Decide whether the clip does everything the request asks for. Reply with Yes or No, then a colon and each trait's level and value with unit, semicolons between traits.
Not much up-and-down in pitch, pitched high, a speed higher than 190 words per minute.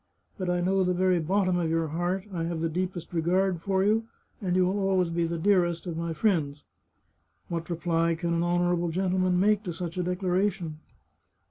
No: narrow, 1.9 semitones; medium, 175 Hz; fast, 205 wpm